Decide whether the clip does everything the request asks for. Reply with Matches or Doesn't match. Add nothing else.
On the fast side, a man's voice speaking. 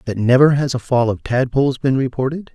Matches